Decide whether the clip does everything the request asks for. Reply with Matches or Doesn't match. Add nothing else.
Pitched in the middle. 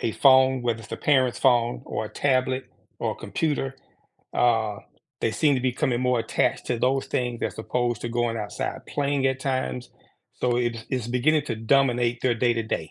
Doesn't match